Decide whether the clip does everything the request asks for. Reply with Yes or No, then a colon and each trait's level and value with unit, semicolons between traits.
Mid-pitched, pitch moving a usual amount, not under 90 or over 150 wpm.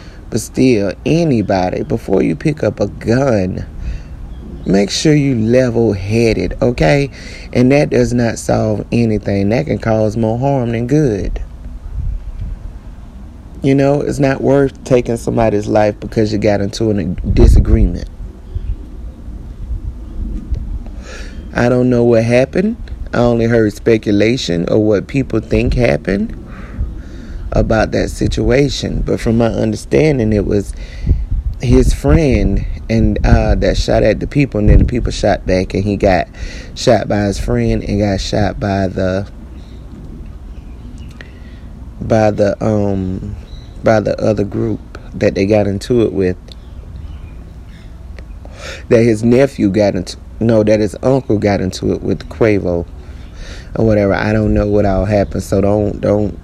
No: low, 105 Hz; average, 4.4 semitones; average, 140 wpm